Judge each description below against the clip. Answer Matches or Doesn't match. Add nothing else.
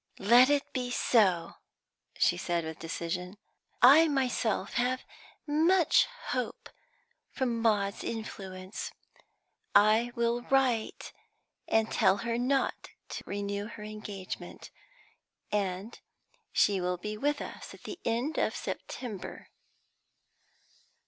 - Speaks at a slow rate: Matches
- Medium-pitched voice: Doesn't match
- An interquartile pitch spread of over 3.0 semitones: Matches